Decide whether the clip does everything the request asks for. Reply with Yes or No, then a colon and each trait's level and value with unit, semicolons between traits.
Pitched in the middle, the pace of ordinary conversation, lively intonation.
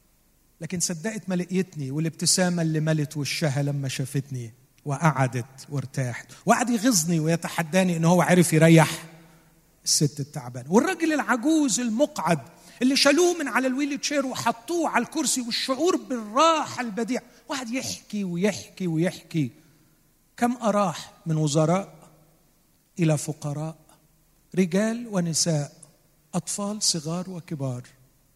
Yes: medium, 170 Hz; average, 110 wpm; wide, 7.0 semitones